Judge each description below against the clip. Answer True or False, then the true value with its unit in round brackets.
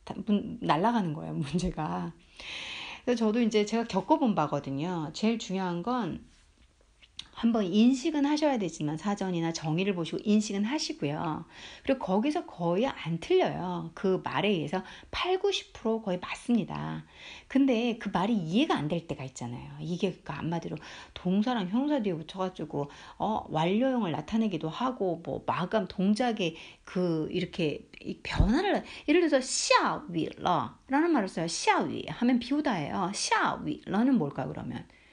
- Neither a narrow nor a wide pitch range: False (6.6 semitones)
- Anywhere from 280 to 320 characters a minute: True (305 characters per minute)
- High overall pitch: True (200 Hz)